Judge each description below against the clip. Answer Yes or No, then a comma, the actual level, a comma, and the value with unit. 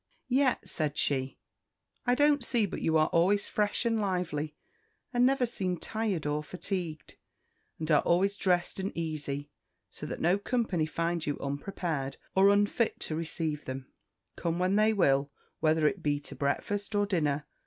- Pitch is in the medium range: Yes, medium, 175 Hz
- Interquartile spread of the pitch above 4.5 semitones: Yes, average, 5.2 semitones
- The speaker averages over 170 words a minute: No, average, 165 wpm